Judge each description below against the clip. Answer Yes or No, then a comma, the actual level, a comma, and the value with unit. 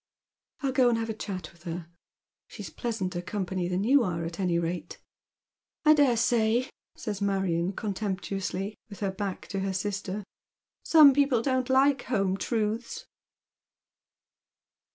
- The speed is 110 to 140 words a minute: No, average, 155 wpm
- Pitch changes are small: No, average, 4.3 semitones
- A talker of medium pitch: No, high, 200 Hz